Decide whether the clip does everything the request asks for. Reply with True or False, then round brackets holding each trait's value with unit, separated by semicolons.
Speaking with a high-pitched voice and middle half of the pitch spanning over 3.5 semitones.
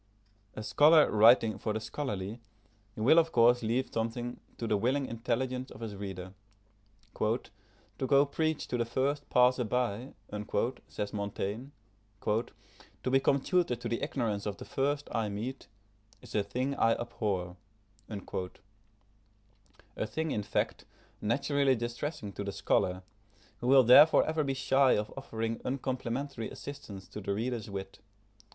False (115 Hz; 4.3 semitones)